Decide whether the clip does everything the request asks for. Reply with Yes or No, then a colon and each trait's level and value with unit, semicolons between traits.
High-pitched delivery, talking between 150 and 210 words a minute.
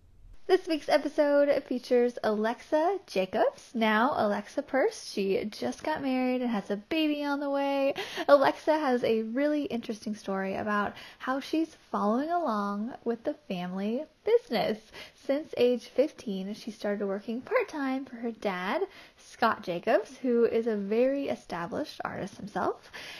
No: very high, 250 Hz; average, 140 wpm